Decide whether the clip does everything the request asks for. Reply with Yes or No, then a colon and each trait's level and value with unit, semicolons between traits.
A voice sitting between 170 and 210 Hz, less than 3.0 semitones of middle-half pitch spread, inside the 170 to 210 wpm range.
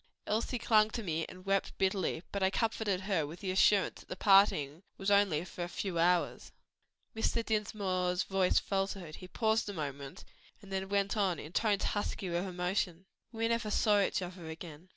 Yes: high, 190 Hz; narrow, 2.6 semitones; average, 180 wpm